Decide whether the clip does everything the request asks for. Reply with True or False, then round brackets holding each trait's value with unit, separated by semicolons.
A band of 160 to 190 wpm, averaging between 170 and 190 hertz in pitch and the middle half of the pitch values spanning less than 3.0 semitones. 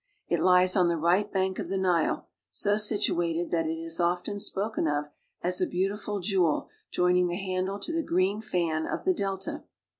True (185 wpm; 185 Hz; 2.5 semitones)